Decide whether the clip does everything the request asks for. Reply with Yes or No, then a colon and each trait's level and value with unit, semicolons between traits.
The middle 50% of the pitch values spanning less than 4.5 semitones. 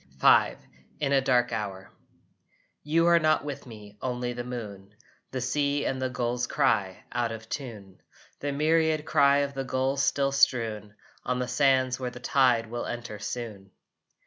Yes: average, 3.5 semitones